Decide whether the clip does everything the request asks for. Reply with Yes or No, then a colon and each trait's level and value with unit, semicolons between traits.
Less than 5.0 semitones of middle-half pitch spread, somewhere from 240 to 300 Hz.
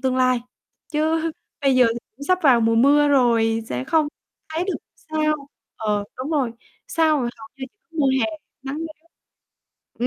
Yes: average, 4.6 semitones; very high, 275 Hz